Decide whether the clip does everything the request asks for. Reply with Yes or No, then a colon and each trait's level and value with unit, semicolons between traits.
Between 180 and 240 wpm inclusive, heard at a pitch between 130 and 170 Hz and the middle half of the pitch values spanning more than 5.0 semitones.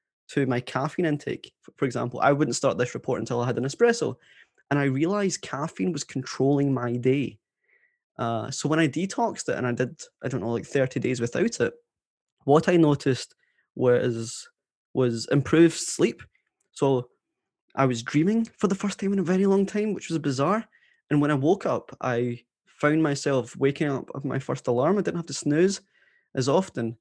Yes: average, 190 wpm; medium, 140 Hz; wide, 5.4 semitones